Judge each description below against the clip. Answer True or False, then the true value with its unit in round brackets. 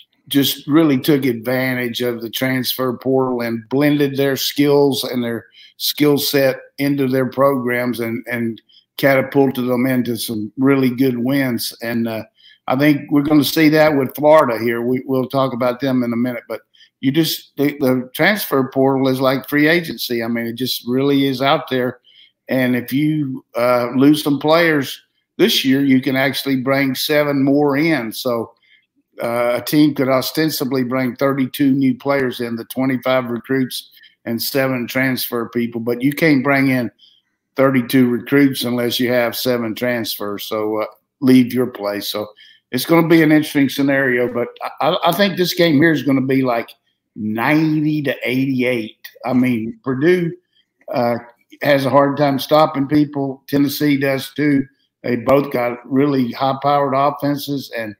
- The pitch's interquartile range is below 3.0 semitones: True (2.5 semitones)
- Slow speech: False (170 wpm)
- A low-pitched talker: True (130 Hz)